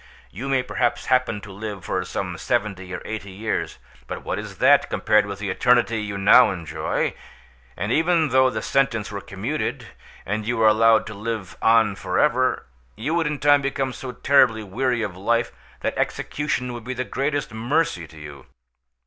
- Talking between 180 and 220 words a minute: Yes, average, 185 wpm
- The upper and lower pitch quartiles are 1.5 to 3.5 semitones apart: No, average, 4.2 semitones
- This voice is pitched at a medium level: No, low, 115 Hz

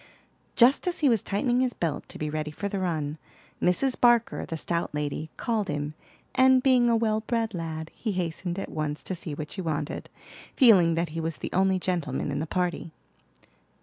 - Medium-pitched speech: Yes, medium, 180 Hz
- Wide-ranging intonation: Yes, wide, 6.5 semitones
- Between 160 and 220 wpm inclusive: Yes, average, 195 wpm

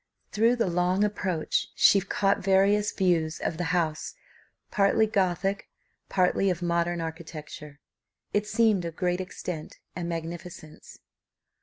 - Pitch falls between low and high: Yes, medium, 180 Hz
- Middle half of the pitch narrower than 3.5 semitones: Yes, average, 2.8 semitones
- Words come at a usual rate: No, slow, 125 wpm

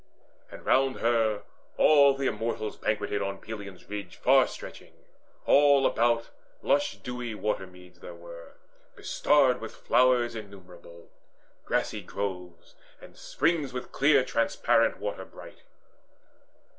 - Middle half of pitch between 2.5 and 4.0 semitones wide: No, average, 4.8 semitones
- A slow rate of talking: Yes, slow, 115 wpm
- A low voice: Yes, low, 110 Hz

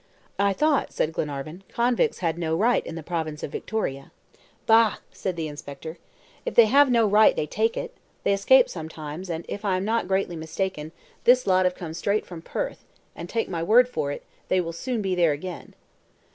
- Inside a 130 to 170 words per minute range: No, average, 200 wpm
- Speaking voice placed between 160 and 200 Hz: Yes, medium, 185 Hz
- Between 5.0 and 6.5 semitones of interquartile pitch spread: Yes, average, 5.3 semitones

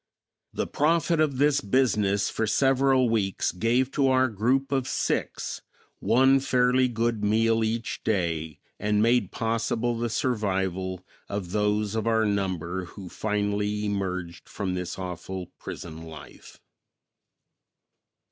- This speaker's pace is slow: Yes, slow, 125 wpm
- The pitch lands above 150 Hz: No, low, 110 Hz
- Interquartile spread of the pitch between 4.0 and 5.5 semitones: Yes, average, 4.6 semitones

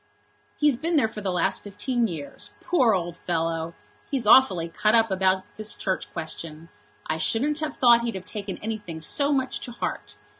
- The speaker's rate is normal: Yes, average, 180 wpm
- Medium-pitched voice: No, high, 210 Hz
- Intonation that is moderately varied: No, wide, 6.1 semitones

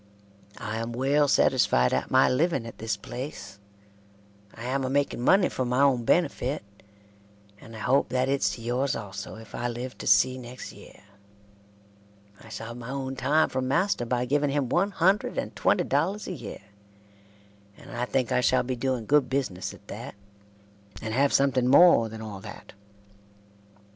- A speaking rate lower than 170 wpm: No, average, 175 wpm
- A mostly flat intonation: No, average, 3.3 semitones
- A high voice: No, low, 130 Hz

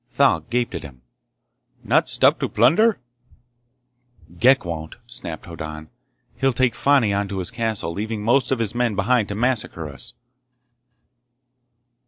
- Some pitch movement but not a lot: No, wide, 6.4 semitones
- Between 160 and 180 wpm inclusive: No, average, 140 wpm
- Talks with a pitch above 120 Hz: No, low, 110 Hz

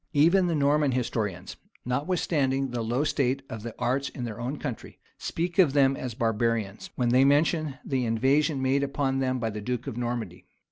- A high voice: No, low, 130 Hz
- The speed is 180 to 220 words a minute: Yes, average, 185 wpm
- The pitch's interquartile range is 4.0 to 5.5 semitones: No, average, 3.2 semitones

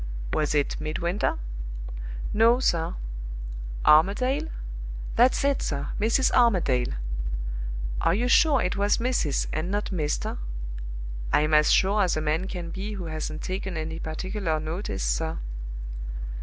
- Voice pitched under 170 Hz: No, medium, 180 Hz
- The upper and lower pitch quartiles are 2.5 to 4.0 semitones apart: No, average, 5.3 semitones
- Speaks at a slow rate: Yes, slow, 130 wpm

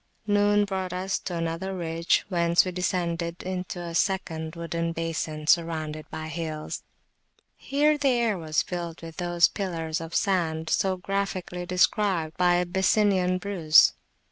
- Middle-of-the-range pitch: Yes, medium, 175 Hz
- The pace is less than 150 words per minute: Yes, average, 140 wpm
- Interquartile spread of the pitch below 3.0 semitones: Yes, narrow, 2.5 semitones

